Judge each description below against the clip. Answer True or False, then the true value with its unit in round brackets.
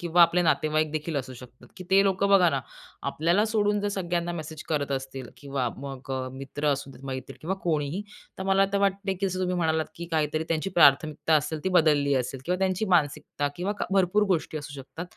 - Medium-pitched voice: True (160 Hz)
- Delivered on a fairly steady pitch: False (4.6 semitones)